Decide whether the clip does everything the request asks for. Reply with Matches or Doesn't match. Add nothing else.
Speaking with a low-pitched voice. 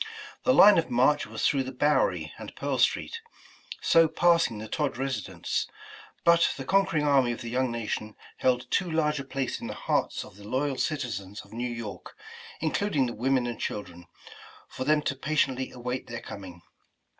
Matches